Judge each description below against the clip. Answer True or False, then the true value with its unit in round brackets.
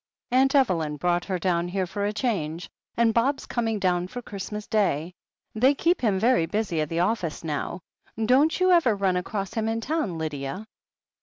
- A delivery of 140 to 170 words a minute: False (180 wpm)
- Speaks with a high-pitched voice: True (200 Hz)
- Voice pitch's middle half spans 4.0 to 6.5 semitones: True (5.1 semitones)